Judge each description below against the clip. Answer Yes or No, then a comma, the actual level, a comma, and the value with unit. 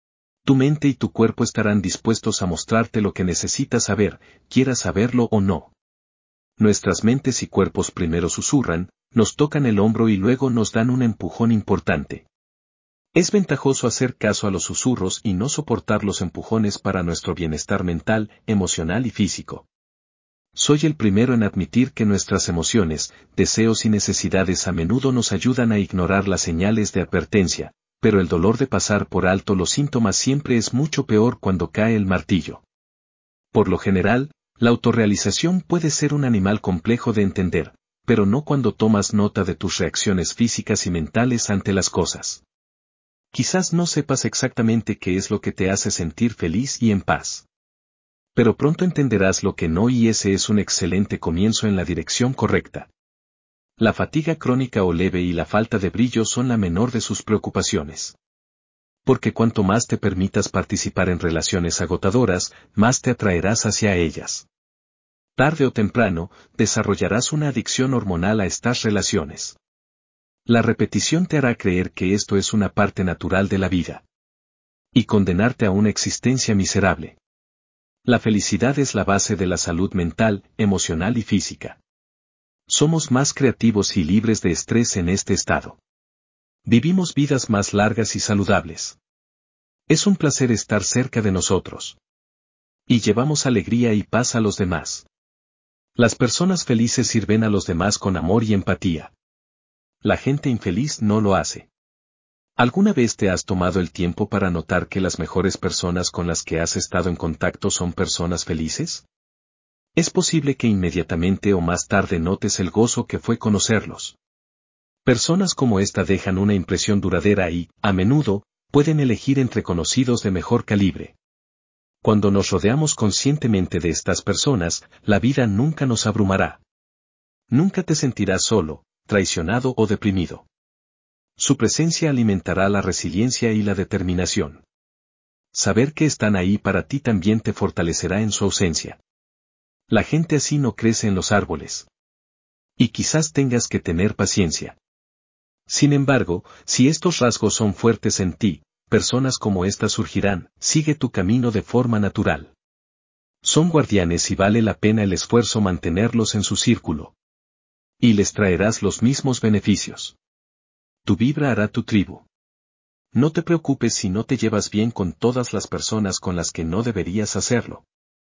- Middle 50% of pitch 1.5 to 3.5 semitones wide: No, average, 4.5 semitones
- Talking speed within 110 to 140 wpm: No, average, 155 wpm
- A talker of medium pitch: No, low, 105 Hz